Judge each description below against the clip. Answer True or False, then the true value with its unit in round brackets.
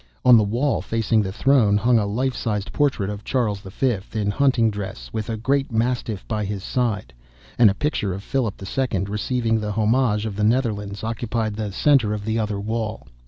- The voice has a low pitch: True (110 Hz)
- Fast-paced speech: False (195 wpm)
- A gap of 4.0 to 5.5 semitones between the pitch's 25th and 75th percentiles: False (2.9 semitones)